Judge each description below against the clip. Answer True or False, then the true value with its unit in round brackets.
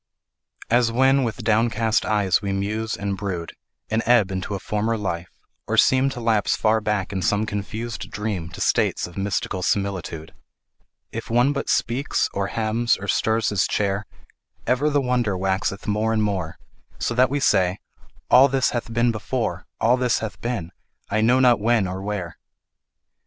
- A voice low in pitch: True (110 Hz)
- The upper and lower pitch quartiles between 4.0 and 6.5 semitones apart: False (3.3 semitones)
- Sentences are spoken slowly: False (170 wpm)